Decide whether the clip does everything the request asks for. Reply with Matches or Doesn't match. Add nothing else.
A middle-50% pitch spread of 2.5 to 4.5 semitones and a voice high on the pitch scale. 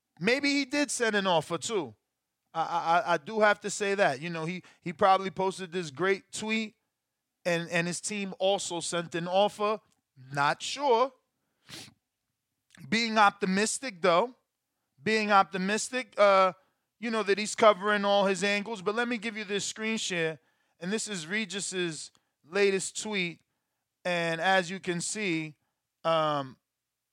Matches